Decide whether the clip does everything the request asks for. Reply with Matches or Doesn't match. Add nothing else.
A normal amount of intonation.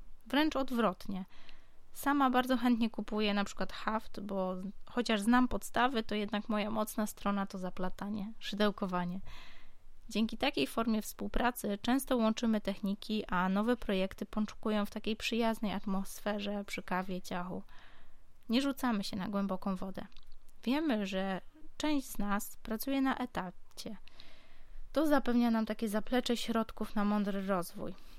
Matches